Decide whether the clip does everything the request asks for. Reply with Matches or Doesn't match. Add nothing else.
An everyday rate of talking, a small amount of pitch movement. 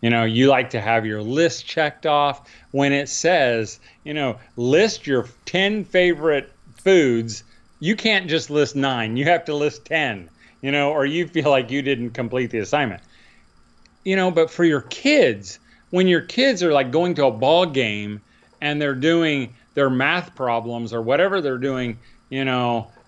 Doesn't match